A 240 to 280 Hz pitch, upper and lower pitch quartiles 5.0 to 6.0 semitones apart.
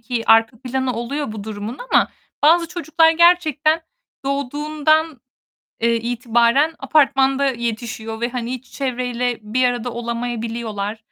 No: high, 245 Hz; average, 3.8 semitones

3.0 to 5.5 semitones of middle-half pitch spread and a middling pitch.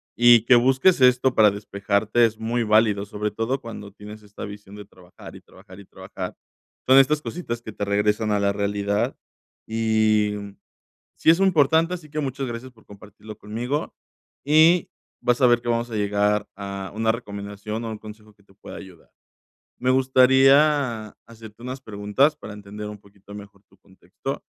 No: average, 3.6 semitones; low, 110 Hz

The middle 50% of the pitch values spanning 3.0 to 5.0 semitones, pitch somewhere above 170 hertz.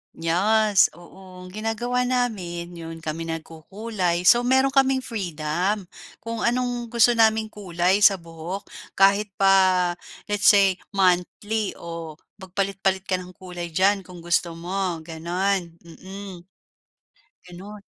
Yes: average, 3.6 semitones; high, 190 Hz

